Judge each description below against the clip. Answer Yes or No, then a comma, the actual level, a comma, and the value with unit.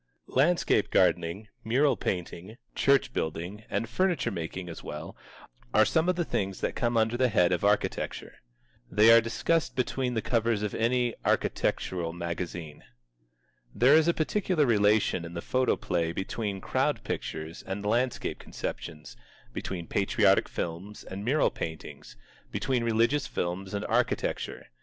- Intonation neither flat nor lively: No, wide, 6.1 semitones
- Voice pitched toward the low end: Yes, low, 110 Hz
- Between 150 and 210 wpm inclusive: No, average, 140 wpm